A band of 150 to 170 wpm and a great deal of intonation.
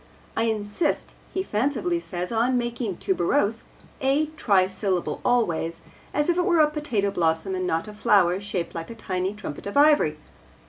Yes: average, 165 wpm; wide, 6.5 semitones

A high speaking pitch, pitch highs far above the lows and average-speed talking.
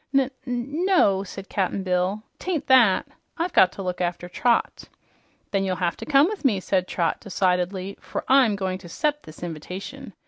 Yes: high, 195 Hz; wide, 6.5 semitones; average, 180 wpm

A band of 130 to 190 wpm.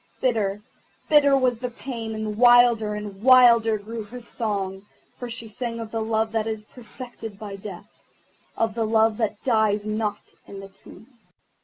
Yes: average, 165 wpm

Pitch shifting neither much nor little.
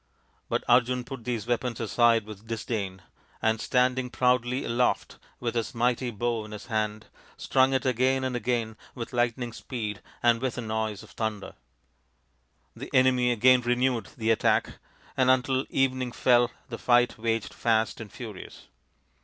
No: narrow, 2.1 semitones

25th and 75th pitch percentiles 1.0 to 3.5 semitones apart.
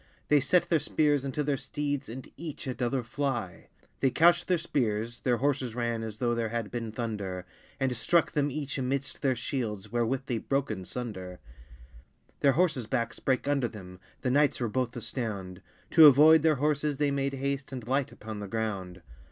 No: average, 4.0 semitones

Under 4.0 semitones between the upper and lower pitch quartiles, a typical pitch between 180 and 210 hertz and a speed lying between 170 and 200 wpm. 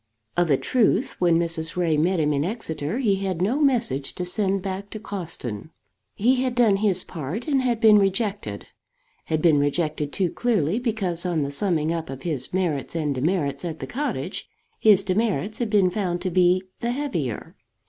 No: average, 5.1 semitones; medium, 185 Hz; average, 185 wpm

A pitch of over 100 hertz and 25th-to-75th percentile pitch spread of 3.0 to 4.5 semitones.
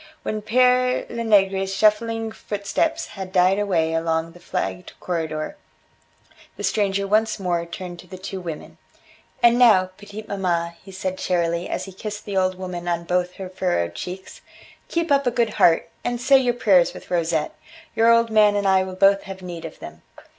Yes: high, 190 Hz; average, 3.6 semitones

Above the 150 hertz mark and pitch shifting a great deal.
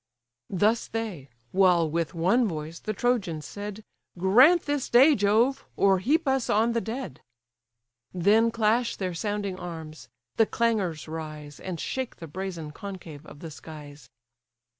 Yes: high, 190 Hz; wide, 5.9 semitones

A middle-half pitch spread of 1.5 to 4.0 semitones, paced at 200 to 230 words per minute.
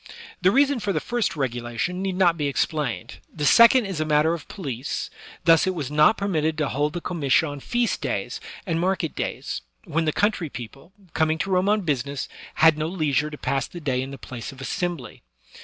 No: average, 4.7 semitones; fast, 205 wpm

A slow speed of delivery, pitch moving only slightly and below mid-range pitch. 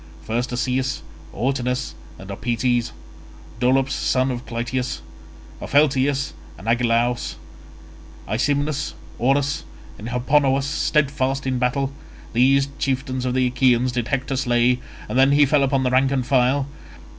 Yes: slow, 125 wpm; narrow, 1.9 semitones; low, 130 Hz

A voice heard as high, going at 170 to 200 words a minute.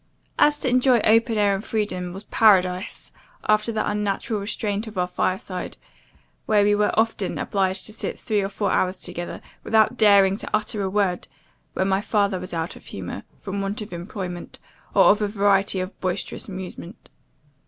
Yes: high, 200 Hz; average, 175 wpm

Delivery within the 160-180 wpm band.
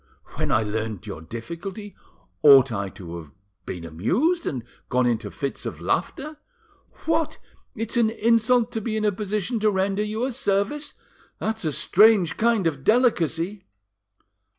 No: average, 150 wpm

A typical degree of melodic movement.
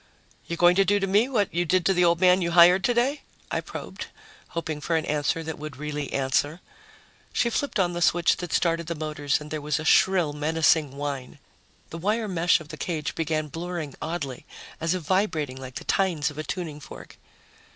Yes: average, 3.2 semitones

